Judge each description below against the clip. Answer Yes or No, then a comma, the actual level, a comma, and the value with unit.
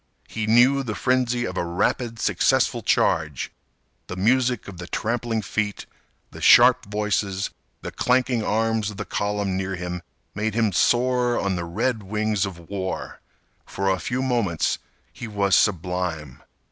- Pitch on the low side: Yes, low, 105 Hz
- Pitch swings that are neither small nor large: Yes, average, 4.2 semitones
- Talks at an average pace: Yes, average, 150 wpm